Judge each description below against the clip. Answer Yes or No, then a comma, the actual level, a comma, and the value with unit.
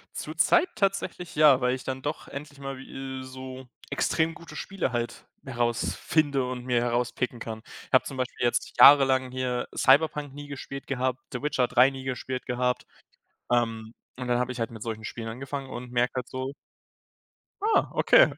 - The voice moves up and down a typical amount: No, narrow, 2.1 semitones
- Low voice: Yes, low, 130 Hz